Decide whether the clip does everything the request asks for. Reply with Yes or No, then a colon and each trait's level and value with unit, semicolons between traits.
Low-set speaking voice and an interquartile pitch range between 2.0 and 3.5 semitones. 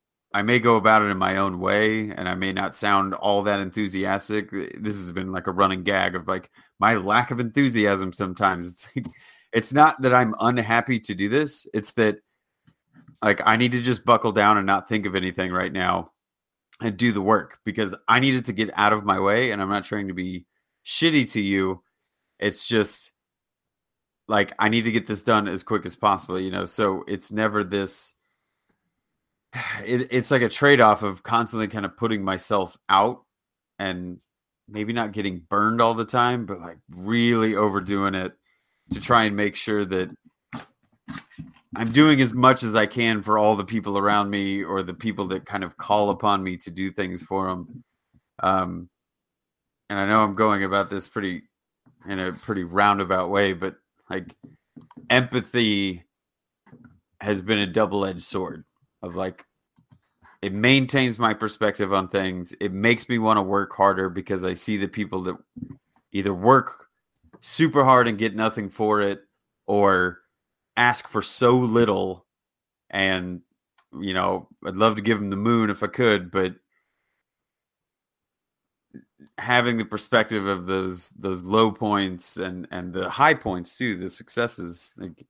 Yes: low, 105 Hz; average, 2.9 semitones